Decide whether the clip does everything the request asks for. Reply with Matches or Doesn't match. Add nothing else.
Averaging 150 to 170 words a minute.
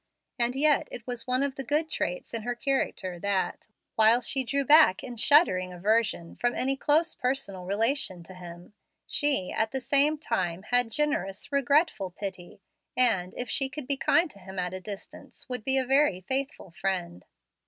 Doesn't match